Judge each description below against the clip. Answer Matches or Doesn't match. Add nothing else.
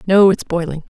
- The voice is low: Doesn't match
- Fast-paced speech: Doesn't match